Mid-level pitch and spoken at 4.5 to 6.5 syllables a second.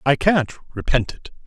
No: medium, 145 Hz; 4.0 syllables/s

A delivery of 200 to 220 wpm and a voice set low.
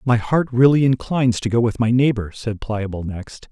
Yes: fast, 205 wpm; low, 120 Hz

